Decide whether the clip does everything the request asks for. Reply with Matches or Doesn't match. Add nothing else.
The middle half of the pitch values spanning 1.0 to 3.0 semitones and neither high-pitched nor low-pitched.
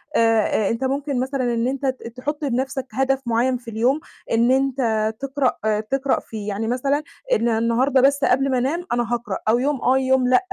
Doesn't match